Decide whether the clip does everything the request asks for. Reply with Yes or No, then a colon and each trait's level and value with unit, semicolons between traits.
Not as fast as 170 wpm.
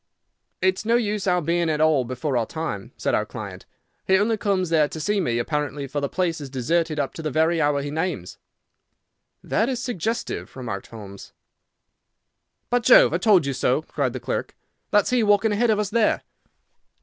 No: average, 195 wpm